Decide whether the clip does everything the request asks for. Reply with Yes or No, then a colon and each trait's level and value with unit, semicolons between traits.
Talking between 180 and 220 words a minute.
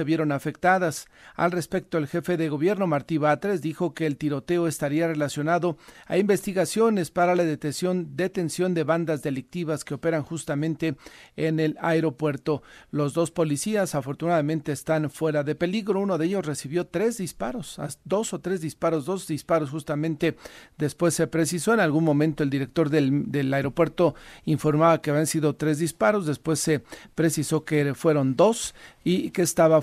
No: average, 160 wpm